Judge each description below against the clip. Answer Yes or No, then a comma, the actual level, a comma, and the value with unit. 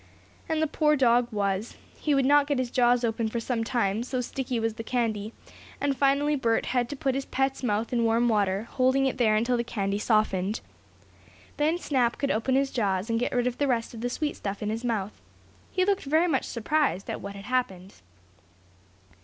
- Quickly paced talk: Yes, fast, 210 wpm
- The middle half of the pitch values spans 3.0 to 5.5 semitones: Yes, average, 3.7 semitones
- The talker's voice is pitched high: Yes, high, 240 Hz